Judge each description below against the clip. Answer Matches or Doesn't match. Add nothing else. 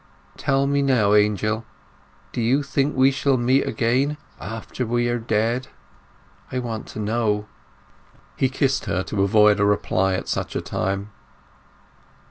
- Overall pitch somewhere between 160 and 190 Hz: Doesn't match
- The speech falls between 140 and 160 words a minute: Matches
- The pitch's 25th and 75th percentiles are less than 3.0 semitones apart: Doesn't match